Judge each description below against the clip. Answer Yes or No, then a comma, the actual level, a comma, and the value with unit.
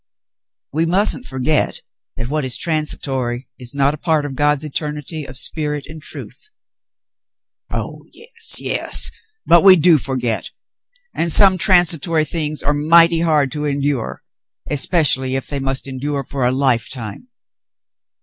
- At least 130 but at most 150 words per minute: Yes, average, 140 wpm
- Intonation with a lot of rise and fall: No, average, 3.5 semitones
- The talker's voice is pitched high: No, medium, 150 Hz